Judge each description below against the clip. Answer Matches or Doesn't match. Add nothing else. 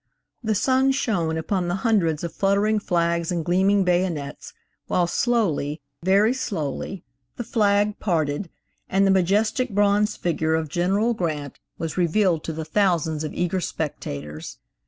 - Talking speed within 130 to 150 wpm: Matches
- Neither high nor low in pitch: Matches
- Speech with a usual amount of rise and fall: Matches